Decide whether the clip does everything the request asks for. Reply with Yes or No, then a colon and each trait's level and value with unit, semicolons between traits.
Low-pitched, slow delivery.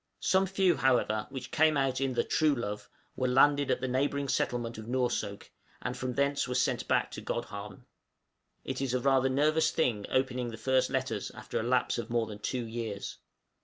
No: low, 130 Hz; average, 190 wpm